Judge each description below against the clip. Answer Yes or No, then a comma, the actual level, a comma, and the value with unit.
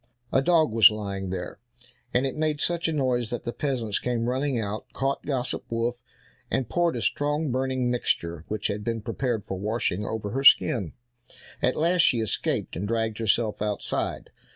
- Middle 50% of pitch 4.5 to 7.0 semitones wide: No, average, 4.0 semitones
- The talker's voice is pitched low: Yes, low, 120 Hz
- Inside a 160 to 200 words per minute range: Yes, average, 175 wpm